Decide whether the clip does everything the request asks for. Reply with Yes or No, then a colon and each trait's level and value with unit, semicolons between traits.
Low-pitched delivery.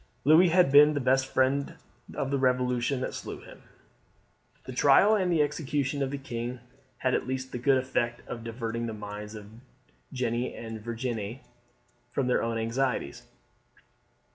Yes: low, 130 Hz